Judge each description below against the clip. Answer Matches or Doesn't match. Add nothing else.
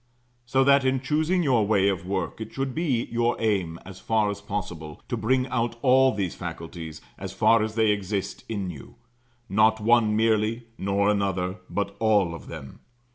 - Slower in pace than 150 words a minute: Doesn't match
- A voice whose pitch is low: Matches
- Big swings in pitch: Doesn't match